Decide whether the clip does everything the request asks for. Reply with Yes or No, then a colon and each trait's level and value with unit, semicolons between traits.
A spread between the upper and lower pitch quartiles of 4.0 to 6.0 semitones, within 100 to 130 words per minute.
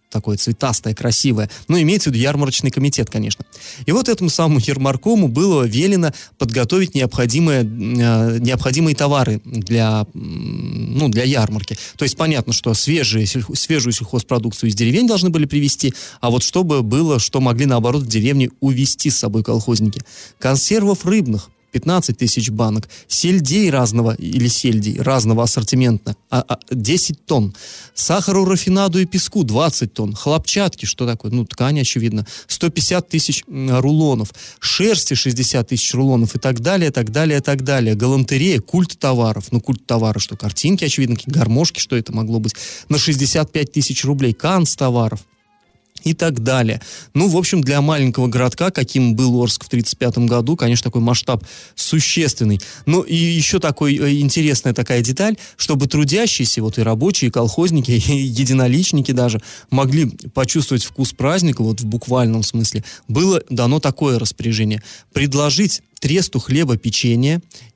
No: average, 4.7 semitones; average, 145 wpm